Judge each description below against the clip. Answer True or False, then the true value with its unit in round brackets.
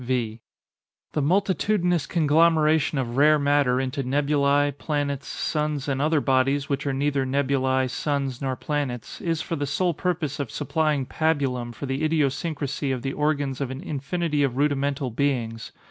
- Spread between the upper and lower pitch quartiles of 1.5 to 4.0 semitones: True (2.4 semitones)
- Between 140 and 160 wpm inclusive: True (155 wpm)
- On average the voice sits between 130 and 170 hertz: True (140 Hz)